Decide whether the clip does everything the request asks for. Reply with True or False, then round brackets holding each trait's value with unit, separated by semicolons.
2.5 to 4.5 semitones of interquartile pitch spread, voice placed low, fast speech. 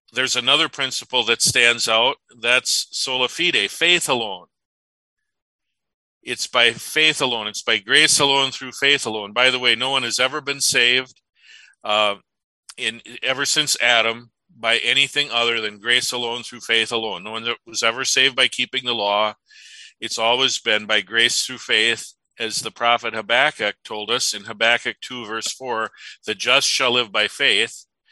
False (3.0 semitones; 125 Hz; 170 wpm)